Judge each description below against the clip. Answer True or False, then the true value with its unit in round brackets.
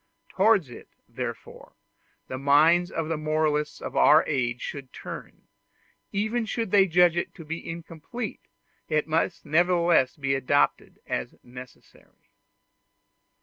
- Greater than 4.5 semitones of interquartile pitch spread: False (3.7 semitones)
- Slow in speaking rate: True (125 wpm)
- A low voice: False (160 Hz)